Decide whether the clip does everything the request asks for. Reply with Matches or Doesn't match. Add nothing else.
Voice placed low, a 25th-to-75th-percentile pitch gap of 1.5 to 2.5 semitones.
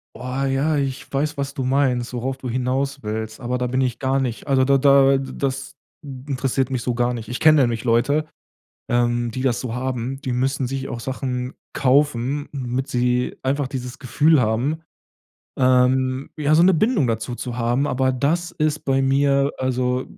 Matches